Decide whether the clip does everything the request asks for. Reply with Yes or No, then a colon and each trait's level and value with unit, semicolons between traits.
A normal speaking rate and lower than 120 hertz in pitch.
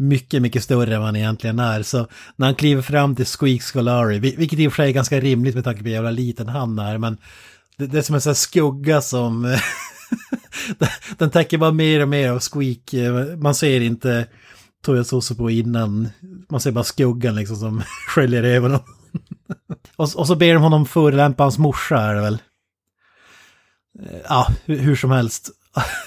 No: average, 180 wpm; low, 130 Hz